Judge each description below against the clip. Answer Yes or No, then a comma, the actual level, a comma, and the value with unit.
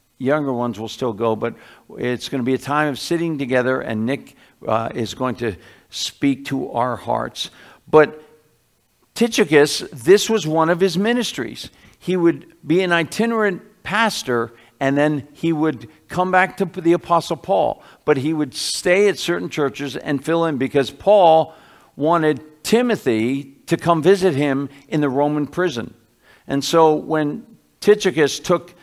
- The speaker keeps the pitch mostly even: No, average, 4.4 semitones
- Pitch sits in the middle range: Yes, medium, 155 Hz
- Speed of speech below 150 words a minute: No, average, 160 wpm